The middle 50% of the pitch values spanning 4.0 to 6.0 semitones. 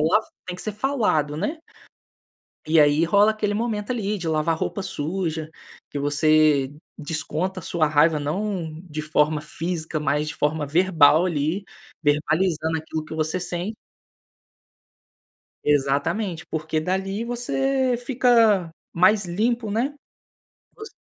Yes: average, 5.2 semitones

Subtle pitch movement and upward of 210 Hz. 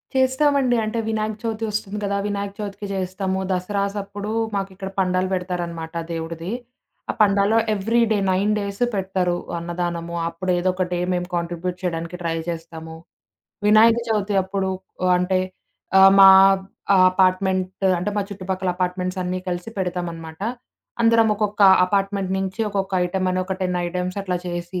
No: narrow, 2.1 semitones; high, 190 Hz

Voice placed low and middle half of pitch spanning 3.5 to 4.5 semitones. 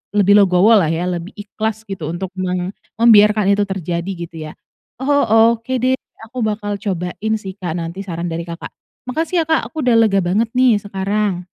No: high, 200 Hz; average, 3.9 semitones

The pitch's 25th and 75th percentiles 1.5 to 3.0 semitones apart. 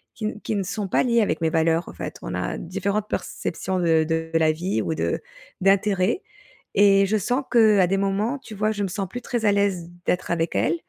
No: average, 3.7 semitones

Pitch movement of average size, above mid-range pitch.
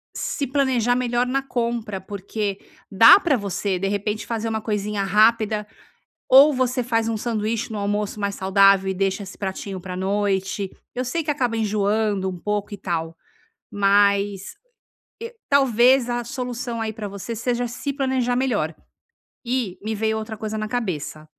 Yes: average, 3.4 semitones; high, 215 Hz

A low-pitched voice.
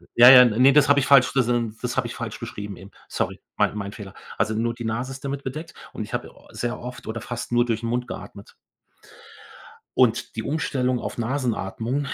Yes: low, 120 Hz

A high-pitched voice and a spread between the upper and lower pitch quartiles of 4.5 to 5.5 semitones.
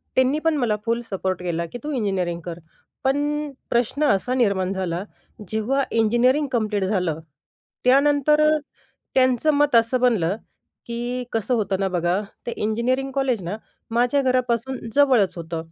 Yes: high, 235 Hz; average, 5.2 semitones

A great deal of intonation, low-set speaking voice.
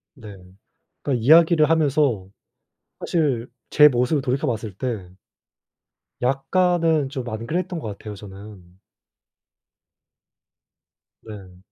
Yes: wide, 6.2 semitones; low, 130 Hz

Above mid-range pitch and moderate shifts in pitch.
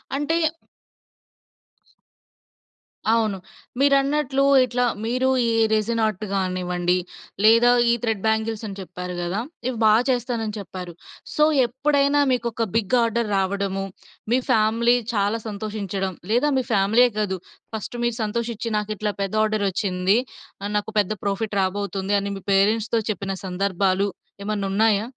Yes: high, 215 Hz; average, 3.2 semitones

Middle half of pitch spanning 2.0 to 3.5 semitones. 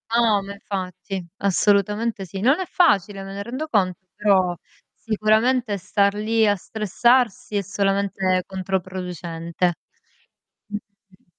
Yes: narrow, 2.6 semitones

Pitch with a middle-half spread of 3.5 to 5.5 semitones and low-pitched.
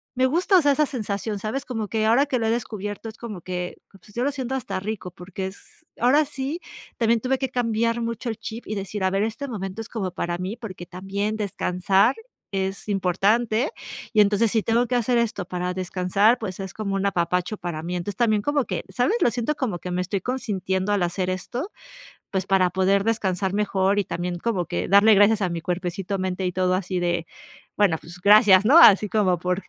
No: average, 3.8 semitones; high, 205 Hz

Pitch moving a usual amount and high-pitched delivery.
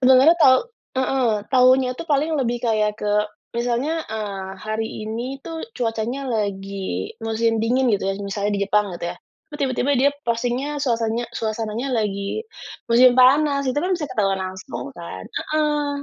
Yes: average, 4.2 semitones; high, 235 Hz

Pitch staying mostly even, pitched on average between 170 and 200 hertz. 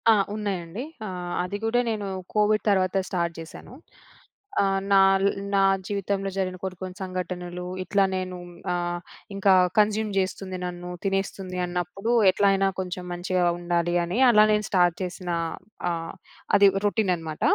Yes: narrow, 1.9 semitones; medium, 185 Hz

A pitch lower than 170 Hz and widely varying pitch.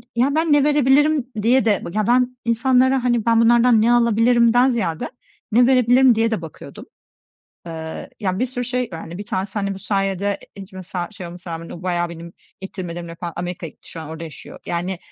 No: high, 215 Hz; wide, 5.9 semitones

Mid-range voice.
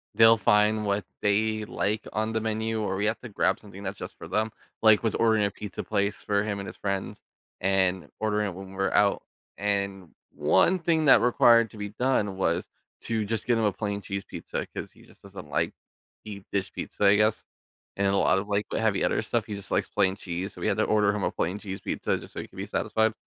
No: low, 105 Hz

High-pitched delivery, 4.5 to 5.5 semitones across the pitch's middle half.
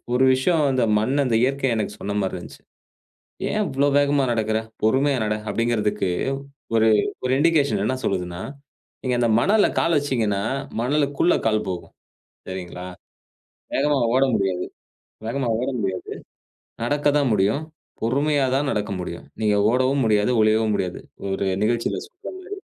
No: low, 120 Hz; average, 5.1 semitones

